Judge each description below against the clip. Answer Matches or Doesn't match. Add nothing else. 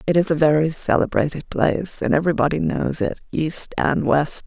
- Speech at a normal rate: Matches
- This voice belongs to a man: Doesn't match